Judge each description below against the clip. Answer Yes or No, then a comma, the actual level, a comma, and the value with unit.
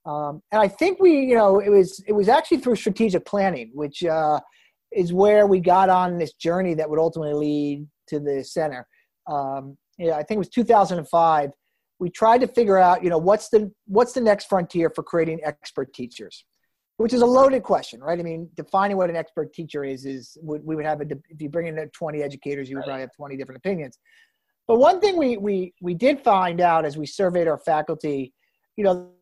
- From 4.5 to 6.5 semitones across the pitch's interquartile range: Yes, average, 5.3 semitones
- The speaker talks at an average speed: No, fast, 220 wpm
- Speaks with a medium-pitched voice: Yes, medium, 170 Hz